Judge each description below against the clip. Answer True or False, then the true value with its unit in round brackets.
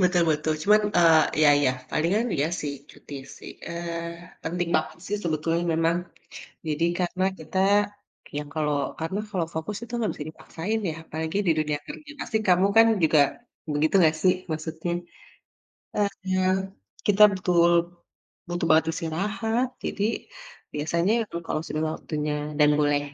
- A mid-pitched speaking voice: True (165 Hz)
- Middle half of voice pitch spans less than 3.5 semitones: True (2.9 semitones)